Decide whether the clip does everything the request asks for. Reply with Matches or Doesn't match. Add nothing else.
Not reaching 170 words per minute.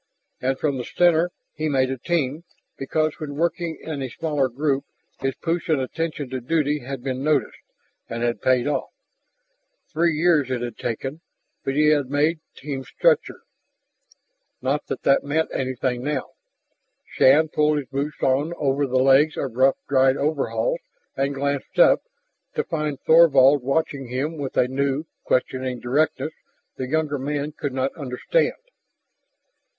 Matches